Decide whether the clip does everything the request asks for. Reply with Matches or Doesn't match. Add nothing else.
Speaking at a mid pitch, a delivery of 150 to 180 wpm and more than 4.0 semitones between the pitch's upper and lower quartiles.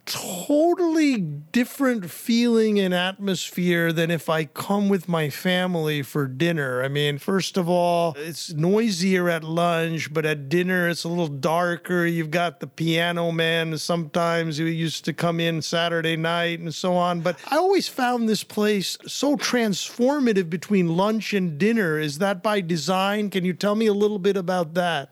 Doesn't match